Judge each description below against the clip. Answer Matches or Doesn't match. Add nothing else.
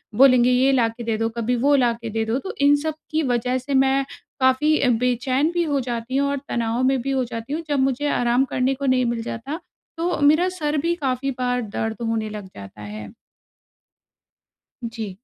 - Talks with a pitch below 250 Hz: Doesn't match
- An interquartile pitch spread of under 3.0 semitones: Doesn't match